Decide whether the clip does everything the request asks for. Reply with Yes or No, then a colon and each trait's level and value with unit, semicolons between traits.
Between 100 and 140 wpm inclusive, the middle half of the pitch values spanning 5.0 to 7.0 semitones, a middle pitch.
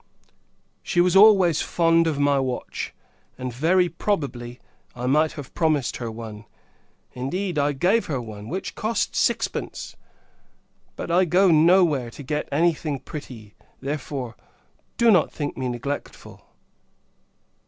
Yes: slow, 135 wpm; average, 5.3 semitones; medium, 150 Hz